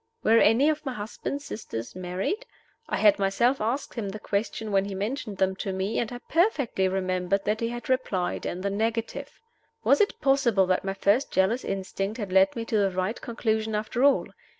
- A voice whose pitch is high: Yes, high, 215 Hz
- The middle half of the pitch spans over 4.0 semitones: No, average, 3.7 semitones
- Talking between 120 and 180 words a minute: No, average, 195 wpm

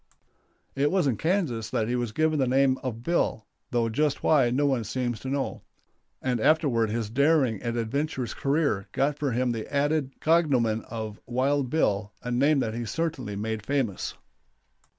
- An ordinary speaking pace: Yes, average, 170 wpm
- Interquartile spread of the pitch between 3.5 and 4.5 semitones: Yes, average, 4.2 semitones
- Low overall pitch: Yes, low, 130 Hz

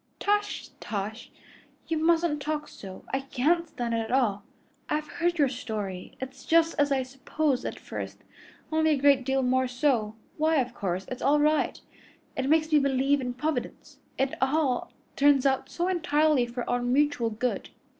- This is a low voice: No, very high, 275 Hz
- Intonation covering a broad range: No, average, 3.8 semitones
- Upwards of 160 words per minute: Yes, average, 170 wpm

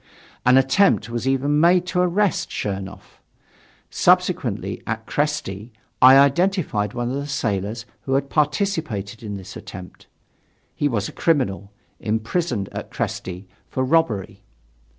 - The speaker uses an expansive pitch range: Yes, wide, 6.5 semitones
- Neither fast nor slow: No, slow, 130 wpm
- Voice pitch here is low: Yes, low, 130 Hz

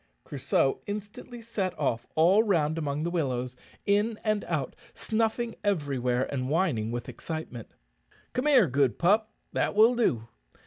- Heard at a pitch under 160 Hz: No, medium, 170 Hz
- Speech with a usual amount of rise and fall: No, wide, 8.1 semitones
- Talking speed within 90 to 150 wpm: Yes, average, 140 wpm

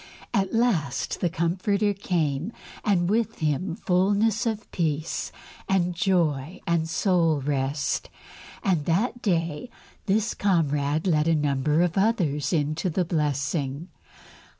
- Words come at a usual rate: No, slow, 120 wpm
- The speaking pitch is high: No, medium, 170 Hz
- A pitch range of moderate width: Yes, average, 4.5 semitones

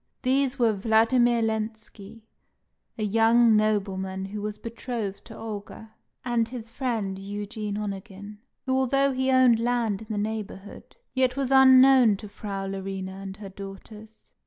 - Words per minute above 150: No, average, 140 wpm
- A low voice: No, high, 220 Hz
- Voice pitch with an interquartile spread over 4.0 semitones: No, average, 3.2 semitones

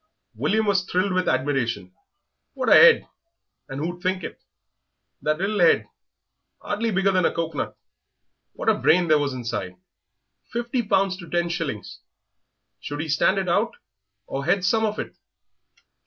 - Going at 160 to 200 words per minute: No, average, 150 wpm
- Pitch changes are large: No, average, 5.0 semitones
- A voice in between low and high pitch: Yes, medium, 175 Hz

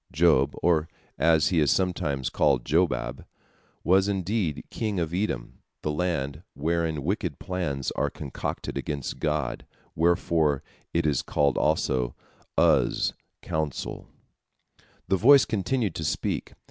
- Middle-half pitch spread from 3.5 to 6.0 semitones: Yes, average, 4.1 semitones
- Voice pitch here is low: Yes, very low, 80 Hz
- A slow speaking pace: Yes, slow, 125 wpm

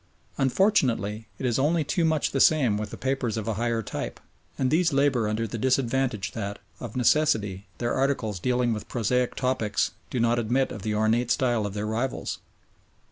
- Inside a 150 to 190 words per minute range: Yes, average, 185 wpm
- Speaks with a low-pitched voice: Yes, low, 120 Hz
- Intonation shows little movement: No, average, 3.5 semitones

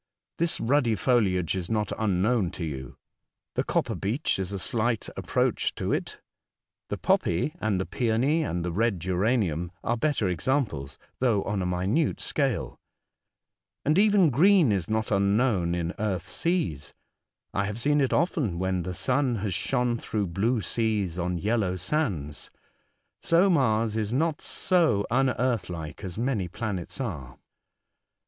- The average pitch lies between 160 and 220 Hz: No, low, 110 Hz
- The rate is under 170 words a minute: Yes, average, 150 wpm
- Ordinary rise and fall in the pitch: No, wide, 6.0 semitones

